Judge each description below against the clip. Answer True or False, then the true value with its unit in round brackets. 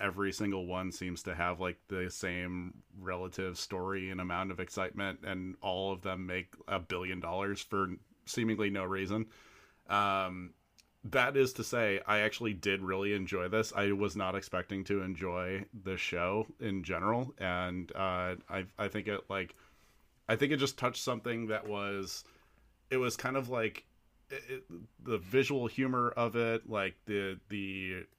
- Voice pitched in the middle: False (100 Hz)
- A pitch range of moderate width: True (3.0 semitones)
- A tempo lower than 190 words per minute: True (165 wpm)